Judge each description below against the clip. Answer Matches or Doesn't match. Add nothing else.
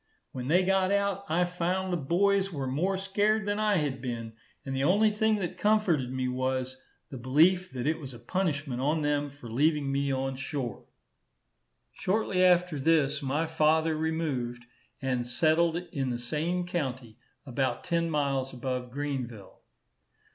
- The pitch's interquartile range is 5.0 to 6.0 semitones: Matches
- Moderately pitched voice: Matches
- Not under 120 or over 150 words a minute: Doesn't match